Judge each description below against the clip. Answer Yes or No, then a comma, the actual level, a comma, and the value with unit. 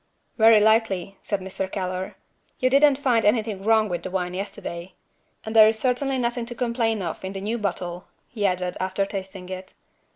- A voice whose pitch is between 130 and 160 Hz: No, high, 205 Hz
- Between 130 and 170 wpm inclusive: No, average, 185 wpm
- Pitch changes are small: No, average, 3.4 semitones